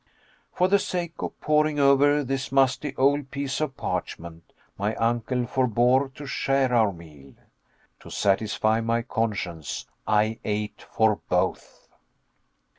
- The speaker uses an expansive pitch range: No, average, 4.6 semitones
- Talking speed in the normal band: No, slow, 125 wpm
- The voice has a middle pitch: No, low, 125 Hz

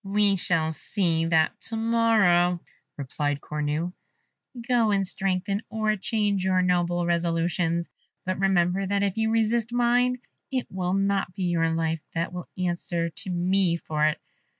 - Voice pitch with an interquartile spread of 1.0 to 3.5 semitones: Yes, average, 3.2 semitones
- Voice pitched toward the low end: No, medium, 185 Hz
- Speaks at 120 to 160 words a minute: Yes, average, 150 wpm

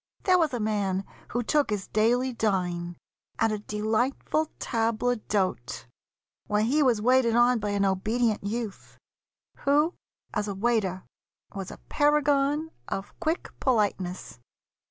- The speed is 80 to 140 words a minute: Yes, slow, 135 wpm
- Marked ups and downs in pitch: No, average, 4.3 semitones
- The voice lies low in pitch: No, high, 225 Hz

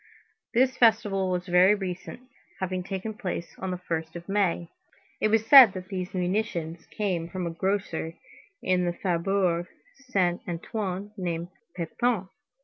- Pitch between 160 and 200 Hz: Yes, medium, 185 Hz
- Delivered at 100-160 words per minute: Yes, average, 140 wpm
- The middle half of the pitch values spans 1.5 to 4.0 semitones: Yes, average, 2.8 semitones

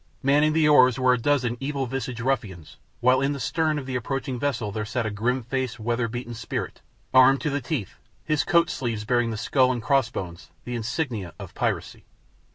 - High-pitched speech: No, low, 125 Hz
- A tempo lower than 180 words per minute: No, average, 200 wpm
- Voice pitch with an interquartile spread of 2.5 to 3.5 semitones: Yes, average, 2.9 semitones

